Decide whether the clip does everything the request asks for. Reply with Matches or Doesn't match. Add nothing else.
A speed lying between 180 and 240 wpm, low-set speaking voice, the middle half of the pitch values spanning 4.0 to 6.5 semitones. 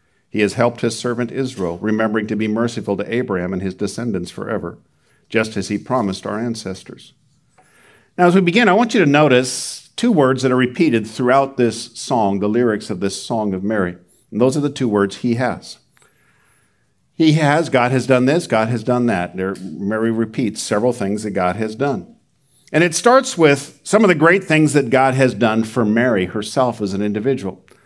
Matches